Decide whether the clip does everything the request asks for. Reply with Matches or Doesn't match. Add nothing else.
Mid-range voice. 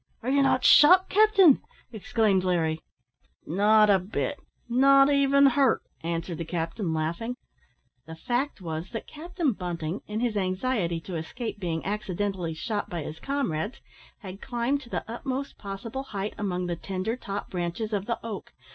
Doesn't match